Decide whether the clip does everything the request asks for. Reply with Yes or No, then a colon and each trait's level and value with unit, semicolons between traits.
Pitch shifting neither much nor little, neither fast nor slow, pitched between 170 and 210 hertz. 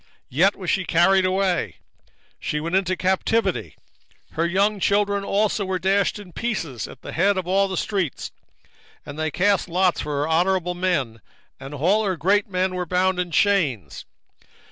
Yes: average, 3.0 semitones; average, 170 wpm; medium, 185 Hz